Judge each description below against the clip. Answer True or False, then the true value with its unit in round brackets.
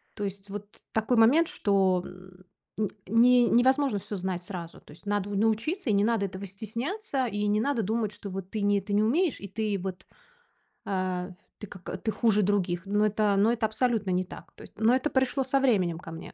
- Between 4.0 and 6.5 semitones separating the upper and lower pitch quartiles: False (3.3 semitones)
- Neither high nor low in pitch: False (210 Hz)